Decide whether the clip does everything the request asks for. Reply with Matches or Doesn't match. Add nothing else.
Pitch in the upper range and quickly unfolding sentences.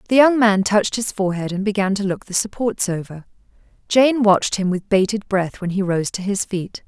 Matches